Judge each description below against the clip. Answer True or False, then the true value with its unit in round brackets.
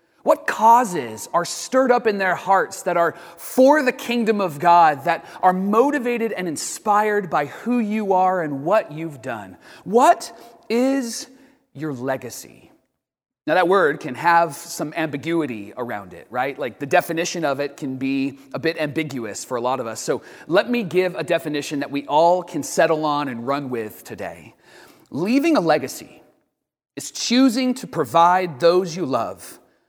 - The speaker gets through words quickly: False (165 wpm)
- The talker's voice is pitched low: False (170 Hz)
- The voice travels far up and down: True (7.3 semitones)